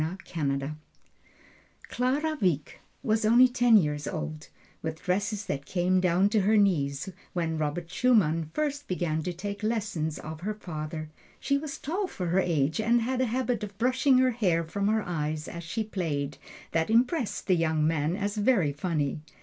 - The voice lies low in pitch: No, medium, 185 Hz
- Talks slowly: No, average, 165 wpm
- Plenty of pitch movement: Yes, wide, 6.1 semitones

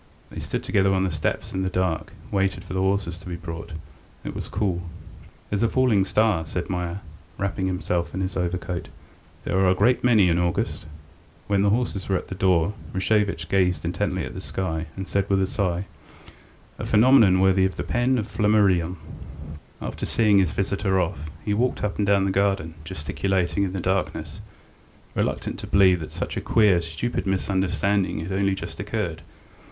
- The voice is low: Yes, very low, 95 Hz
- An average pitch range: No, narrow, 2.2 semitones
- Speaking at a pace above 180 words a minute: Yes, average, 190 wpm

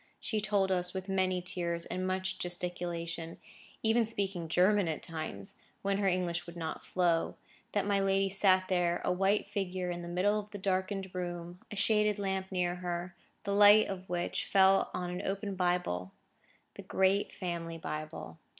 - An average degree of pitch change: No, narrow, 2.0 semitones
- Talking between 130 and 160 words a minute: No, average, 170 wpm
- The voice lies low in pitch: No, medium, 185 Hz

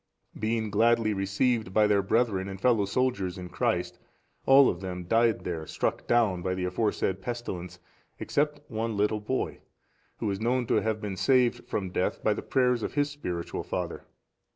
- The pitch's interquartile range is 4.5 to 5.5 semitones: No, average, 4.0 semitones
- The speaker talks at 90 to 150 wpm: No, average, 175 wpm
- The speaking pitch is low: Yes, low, 110 Hz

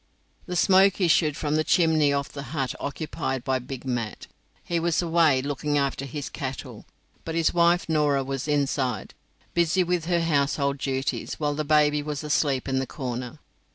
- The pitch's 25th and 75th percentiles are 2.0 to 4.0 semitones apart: Yes, average, 3.2 semitones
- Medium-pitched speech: Yes, medium, 145 Hz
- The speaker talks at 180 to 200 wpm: No, average, 170 wpm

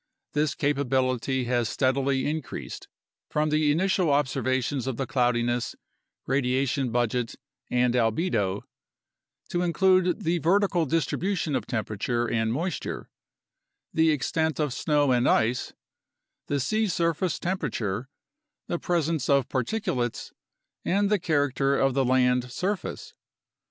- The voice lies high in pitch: No, medium, 140 Hz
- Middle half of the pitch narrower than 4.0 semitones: No, average, 4.9 semitones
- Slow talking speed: Yes, slow, 120 wpm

